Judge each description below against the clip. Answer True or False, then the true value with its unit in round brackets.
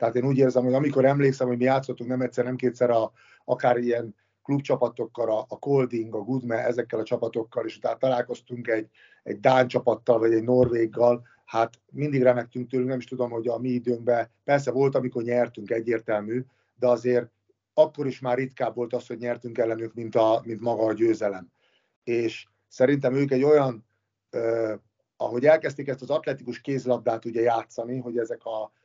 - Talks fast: True (180 wpm)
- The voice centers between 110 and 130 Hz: True (120 Hz)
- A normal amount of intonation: False (2.0 semitones)